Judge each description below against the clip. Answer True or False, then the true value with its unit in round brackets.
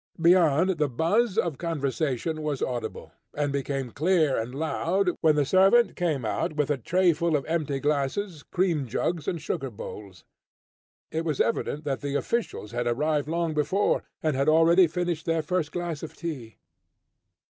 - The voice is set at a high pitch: False (155 Hz)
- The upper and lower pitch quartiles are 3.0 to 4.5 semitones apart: True (3.6 semitones)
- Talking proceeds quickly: False (160 wpm)